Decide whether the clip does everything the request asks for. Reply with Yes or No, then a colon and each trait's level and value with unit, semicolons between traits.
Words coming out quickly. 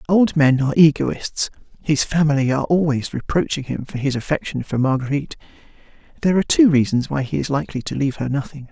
No: average, 185 wpm